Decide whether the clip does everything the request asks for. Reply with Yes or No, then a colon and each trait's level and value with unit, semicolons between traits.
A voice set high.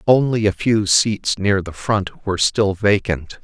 No: low, 100 Hz